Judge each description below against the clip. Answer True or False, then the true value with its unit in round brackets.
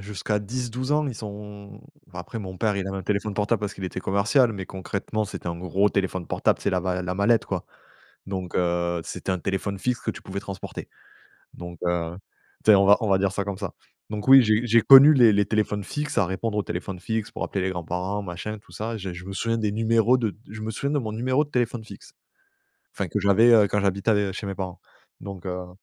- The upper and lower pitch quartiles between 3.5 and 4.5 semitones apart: False (2.9 semitones)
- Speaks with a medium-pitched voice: False (100 Hz)